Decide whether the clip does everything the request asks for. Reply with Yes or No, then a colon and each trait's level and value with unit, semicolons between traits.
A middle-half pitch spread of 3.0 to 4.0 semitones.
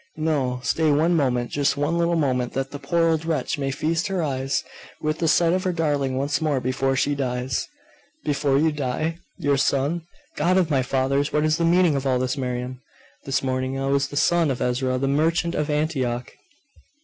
Yes: average, 3.4 semitones